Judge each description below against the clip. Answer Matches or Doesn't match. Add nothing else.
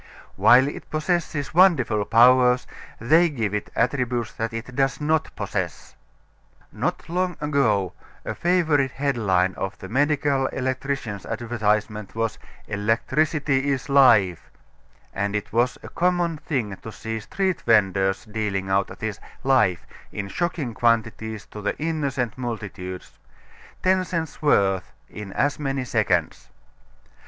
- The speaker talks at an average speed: Doesn't match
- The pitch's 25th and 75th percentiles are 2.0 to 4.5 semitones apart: Doesn't match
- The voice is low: Matches